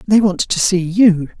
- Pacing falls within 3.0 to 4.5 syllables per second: Yes, 4.2 syllables/s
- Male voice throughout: Yes, male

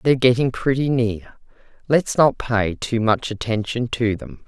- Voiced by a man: No, female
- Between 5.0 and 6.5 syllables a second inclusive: No, 4.4 syllables/s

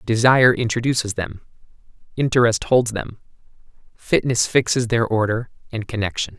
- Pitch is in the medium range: No, low, 115 Hz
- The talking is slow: Yes, slow, 115 wpm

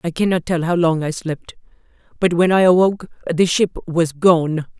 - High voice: No, medium, 170 Hz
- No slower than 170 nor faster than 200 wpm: Yes, average, 190 wpm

